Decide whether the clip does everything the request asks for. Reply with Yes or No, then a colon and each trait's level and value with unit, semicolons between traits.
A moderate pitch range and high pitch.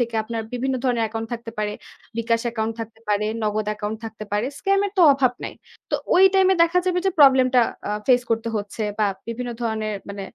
Yes: average, 3.0 semitones; high, 230 Hz